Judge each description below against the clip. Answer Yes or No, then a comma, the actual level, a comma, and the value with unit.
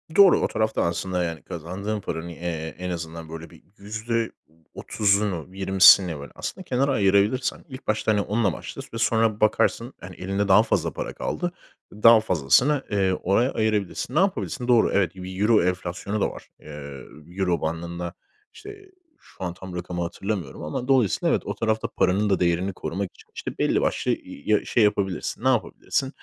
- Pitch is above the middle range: No, low, 100 Hz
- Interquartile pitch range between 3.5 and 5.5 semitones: Yes, average, 4.2 semitones